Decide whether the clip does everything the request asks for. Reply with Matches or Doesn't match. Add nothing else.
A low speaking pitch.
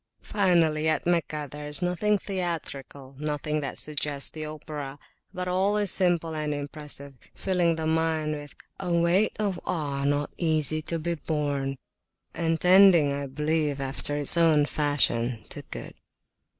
Doesn't match